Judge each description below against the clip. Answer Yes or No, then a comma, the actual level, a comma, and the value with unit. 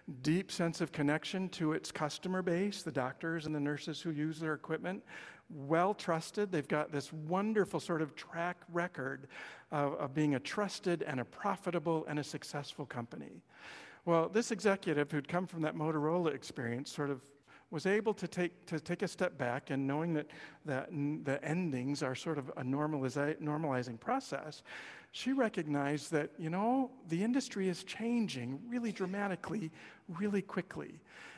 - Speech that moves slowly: No, average, 165 wpm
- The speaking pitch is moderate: Yes, medium, 160 Hz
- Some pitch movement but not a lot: Yes, average, 4.2 semitones